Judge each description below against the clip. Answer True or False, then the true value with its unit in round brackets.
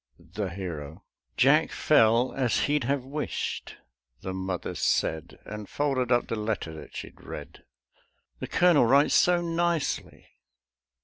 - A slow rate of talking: True (130 wpm)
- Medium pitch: False (120 Hz)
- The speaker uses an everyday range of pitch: False (7.3 semitones)